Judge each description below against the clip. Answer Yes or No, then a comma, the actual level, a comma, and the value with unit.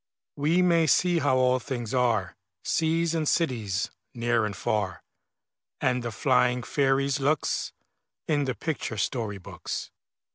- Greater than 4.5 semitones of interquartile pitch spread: Yes, average, 5.1 semitones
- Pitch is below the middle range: Yes, low, 130 Hz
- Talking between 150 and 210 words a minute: No, slow, 135 wpm